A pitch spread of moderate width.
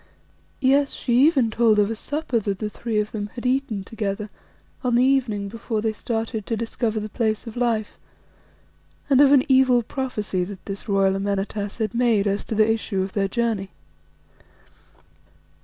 Yes: average, 3.0 semitones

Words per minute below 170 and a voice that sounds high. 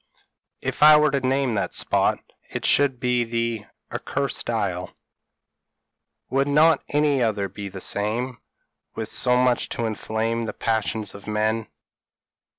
No: average, 150 wpm; low, 115 Hz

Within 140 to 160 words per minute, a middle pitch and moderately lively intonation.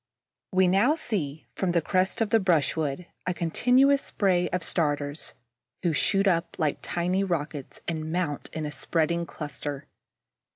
Yes: average, 150 wpm; medium, 170 Hz; average, 3.7 semitones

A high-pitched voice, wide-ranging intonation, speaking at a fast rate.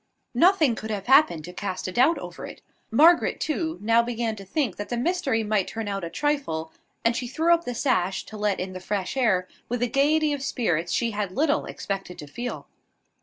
Yes: high, 230 Hz; wide, 6.5 semitones; fast, 215 wpm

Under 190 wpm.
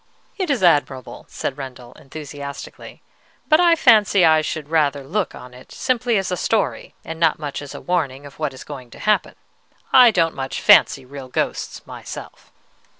Yes: average, 170 wpm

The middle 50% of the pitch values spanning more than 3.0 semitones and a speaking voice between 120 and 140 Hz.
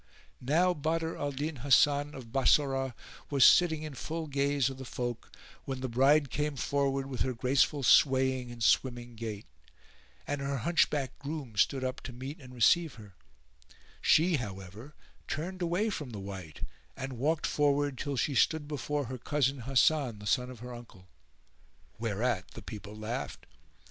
Yes: average, 3.4 semitones; low, 135 Hz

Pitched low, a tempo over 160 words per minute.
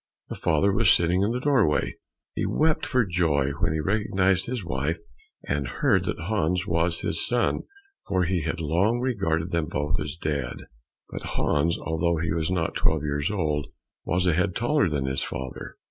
Yes: very low, 85 Hz; average, 180 wpm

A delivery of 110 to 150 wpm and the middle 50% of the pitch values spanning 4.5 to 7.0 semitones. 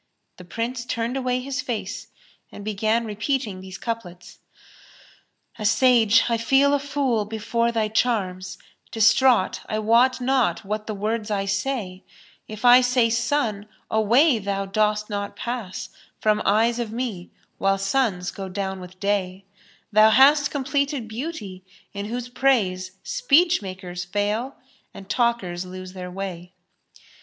No: average, 145 wpm; average, 4.0 semitones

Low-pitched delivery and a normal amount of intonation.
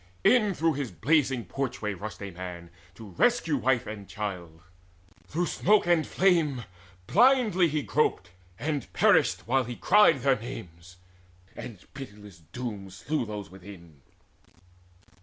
No: low, 120 Hz; wide, 7.9 semitones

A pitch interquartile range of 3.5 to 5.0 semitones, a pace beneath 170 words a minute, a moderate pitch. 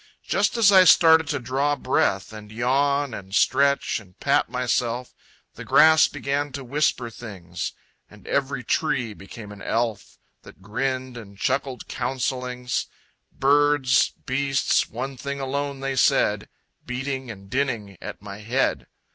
No: average, 3.8 semitones; average, 140 wpm; low, 130 Hz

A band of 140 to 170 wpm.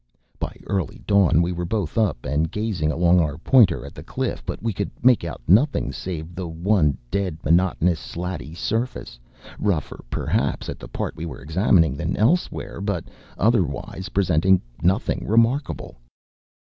Yes: average, 155 wpm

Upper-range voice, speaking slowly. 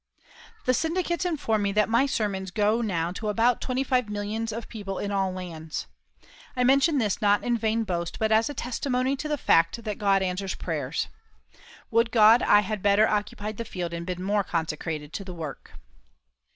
No: high, 210 Hz; average, 190 wpm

